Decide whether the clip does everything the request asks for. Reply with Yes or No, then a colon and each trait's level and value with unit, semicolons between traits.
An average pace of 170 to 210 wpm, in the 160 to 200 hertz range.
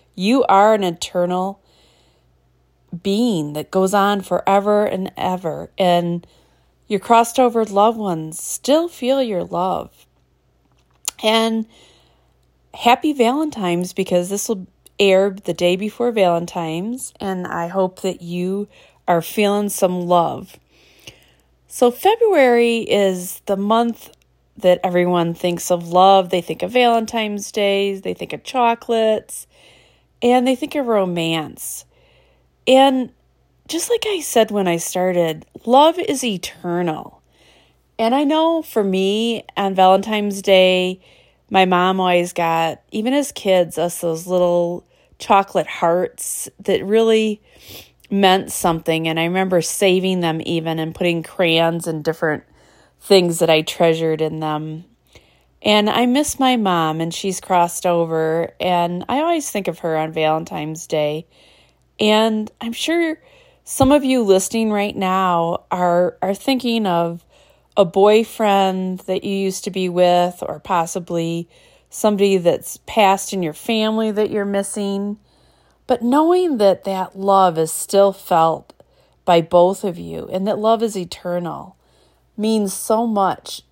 No: slow, 135 wpm; high, 190 Hz